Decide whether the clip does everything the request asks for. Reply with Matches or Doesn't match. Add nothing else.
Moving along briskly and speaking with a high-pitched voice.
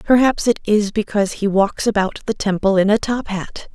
Matches